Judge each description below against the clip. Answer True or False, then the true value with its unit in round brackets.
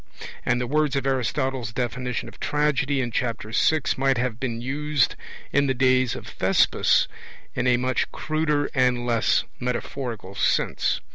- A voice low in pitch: True (130 Hz)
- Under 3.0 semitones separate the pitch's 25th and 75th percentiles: True (2.5 semitones)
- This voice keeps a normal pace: True (150 wpm)